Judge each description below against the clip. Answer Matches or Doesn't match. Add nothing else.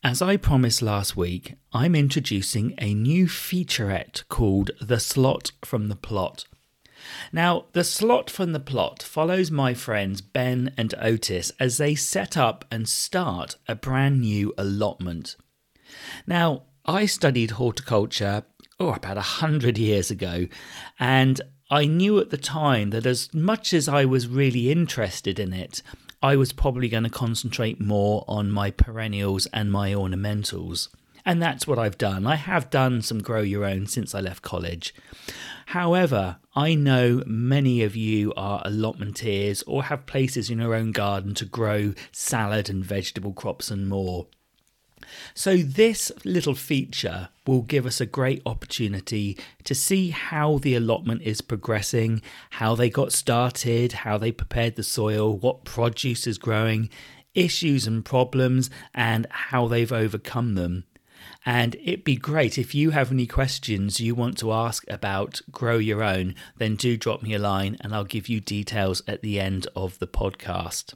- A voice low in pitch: Matches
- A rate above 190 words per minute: Doesn't match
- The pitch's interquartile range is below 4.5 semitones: Doesn't match